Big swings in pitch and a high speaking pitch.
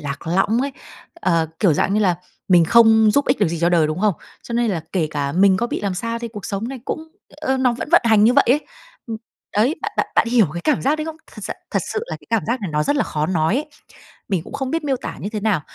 Yes: wide, 6.3 semitones; high, 220 Hz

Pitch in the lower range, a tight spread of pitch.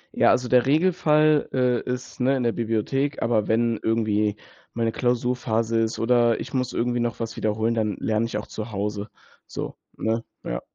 Yes: low, 115 Hz; narrow, 2.3 semitones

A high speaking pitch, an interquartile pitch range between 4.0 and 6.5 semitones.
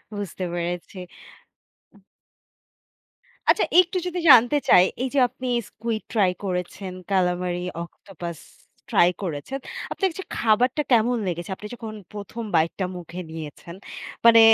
Yes: high, 195 Hz; average, 5.2 semitones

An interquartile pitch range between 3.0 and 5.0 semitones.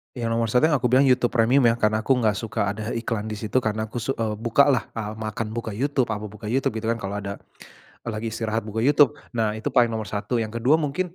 No: narrow, 2.4 semitones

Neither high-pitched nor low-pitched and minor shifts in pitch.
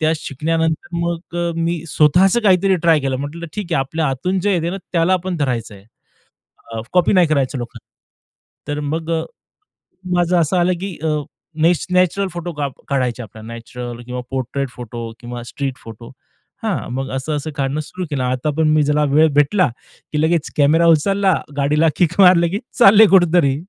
No: medium, 160 Hz; average, 4.6 semitones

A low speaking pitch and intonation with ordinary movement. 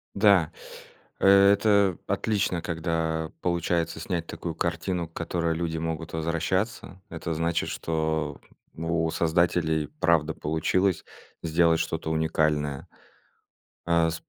No: very low, 85 Hz; narrow, 1.6 semitones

